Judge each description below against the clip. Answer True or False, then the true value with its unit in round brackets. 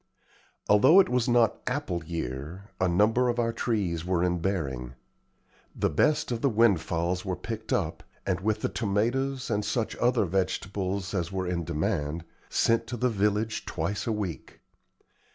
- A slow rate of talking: False (160 wpm)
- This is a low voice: True (100 Hz)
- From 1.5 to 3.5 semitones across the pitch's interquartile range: False (4.7 semitones)